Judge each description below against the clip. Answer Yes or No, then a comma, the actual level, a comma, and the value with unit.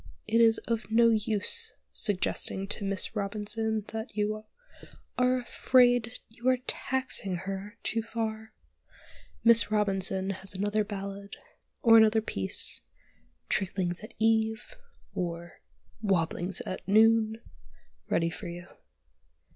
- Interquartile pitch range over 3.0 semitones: No, narrow, 2.6 semitones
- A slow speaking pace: Yes, slow, 115 wpm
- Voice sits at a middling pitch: No, high, 215 Hz